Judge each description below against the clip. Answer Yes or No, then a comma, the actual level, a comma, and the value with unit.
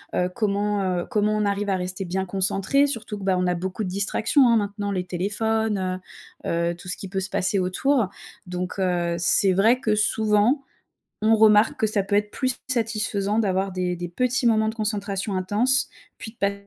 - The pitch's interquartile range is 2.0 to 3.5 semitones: Yes, average, 2.9 semitones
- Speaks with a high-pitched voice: Yes, high, 200 Hz